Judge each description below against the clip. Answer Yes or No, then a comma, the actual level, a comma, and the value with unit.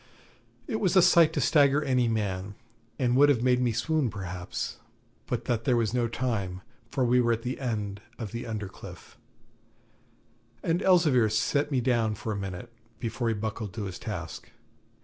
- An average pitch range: Yes, average, 3.7 semitones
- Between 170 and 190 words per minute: Yes, average, 180 wpm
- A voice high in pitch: No, low, 115 Hz